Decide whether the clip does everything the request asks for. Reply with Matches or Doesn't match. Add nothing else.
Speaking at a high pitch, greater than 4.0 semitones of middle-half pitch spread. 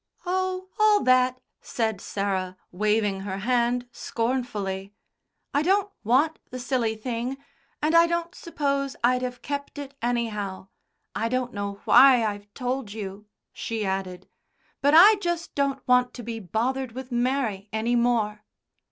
Matches